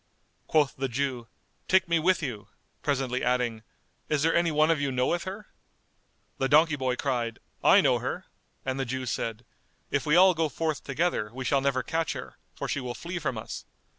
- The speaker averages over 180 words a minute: Yes, average, 195 wpm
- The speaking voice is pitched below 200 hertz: Yes, medium, 140 Hz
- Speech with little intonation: No, average, 4.4 semitones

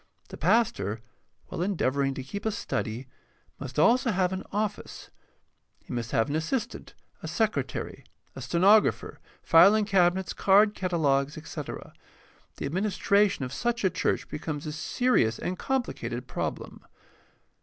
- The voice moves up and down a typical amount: No, wide, 6.9 semitones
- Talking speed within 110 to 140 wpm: Yes, slow, 135 wpm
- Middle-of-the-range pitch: Yes, medium, 175 Hz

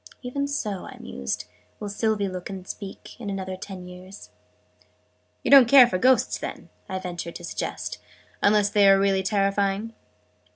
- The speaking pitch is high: Yes, high, 195 Hz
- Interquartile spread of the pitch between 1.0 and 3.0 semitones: Yes, narrow, 2.4 semitones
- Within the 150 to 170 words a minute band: Yes, average, 160 wpm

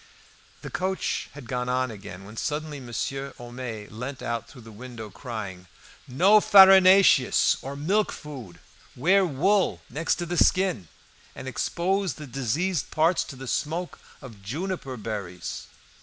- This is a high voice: No, low, 135 Hz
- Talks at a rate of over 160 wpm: No, average, 140 wpm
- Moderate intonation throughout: No, wide, 7.1 semitones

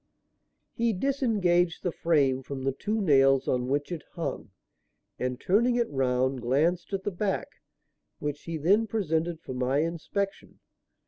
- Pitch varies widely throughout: Yes, wide, 6.5 semitones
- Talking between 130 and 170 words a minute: Yes, average, 145 wpm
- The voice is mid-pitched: Yes, medium, 165 Hz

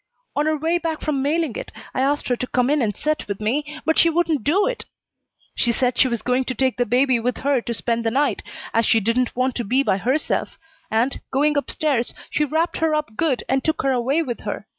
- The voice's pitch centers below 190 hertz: No, very high, 265 Hz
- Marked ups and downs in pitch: No, average, 4.0 semitones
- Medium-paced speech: No, fast, 245 wpm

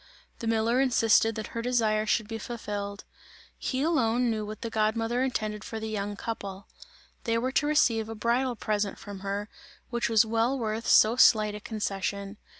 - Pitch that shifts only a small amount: Yes, narrow, 1.9 semitones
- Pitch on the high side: Yes, high, 225 Hz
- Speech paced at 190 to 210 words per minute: No, average, 180 wpm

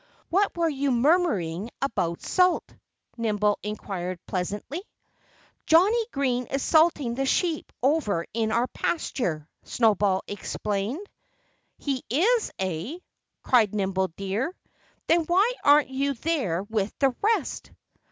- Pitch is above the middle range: Yes, very high, 250 Hz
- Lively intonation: Yes, wide, 8.0 semitones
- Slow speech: Yes, slow, 115 wpm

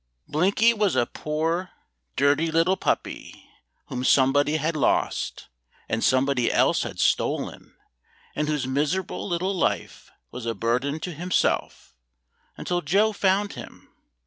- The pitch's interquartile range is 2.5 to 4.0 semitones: No, average, 5.3 semitones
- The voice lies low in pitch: No, medium, 155 Hz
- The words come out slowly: Yes, slow, 125 wpm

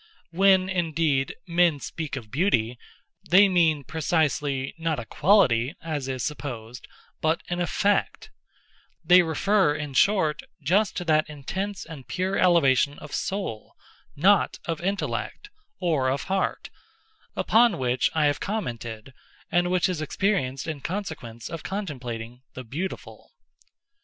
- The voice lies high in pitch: No, medium, 160 Hz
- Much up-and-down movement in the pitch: Yes, wide, 5.8 semitones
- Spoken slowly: Yes, slow, 120 wpm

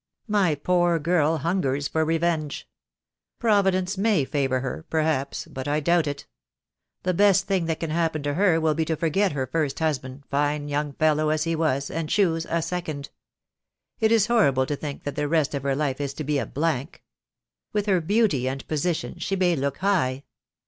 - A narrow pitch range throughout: No, average, 3.8 semitones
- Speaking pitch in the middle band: Yes, medium, 155 Hz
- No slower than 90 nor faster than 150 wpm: No, average, 190 wpm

